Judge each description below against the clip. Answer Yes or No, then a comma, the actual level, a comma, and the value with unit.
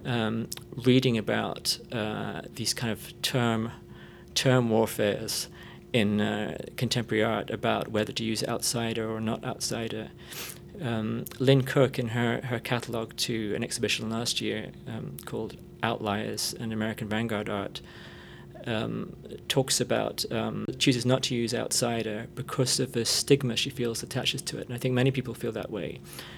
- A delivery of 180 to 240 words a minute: No, average, 150 wpm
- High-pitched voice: No, low, 115 Hz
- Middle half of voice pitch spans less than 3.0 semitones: Yes, narrow, 2.5 semitones